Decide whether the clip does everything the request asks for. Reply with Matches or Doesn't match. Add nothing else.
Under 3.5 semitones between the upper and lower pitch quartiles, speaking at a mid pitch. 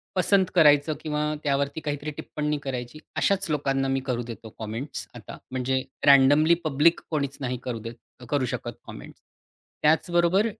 Matches